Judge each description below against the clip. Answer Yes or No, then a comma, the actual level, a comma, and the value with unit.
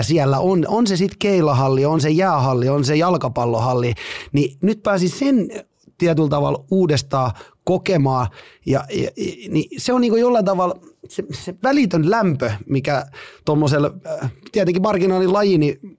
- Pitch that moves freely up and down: Yes, wide, 5.8 semitones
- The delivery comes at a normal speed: Yes, average, 145 wpm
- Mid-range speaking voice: Yes, medium, 165 Hz